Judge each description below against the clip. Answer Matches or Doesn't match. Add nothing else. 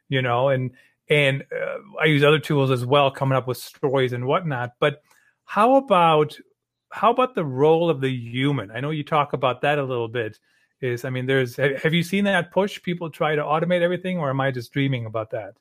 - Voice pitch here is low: Doesn't match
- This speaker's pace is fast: Matches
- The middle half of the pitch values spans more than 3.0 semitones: Matches